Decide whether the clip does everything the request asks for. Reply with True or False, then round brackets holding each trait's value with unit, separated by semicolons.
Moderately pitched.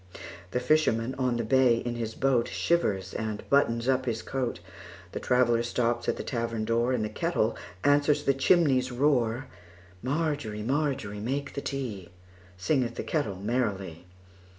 False (120 Hz)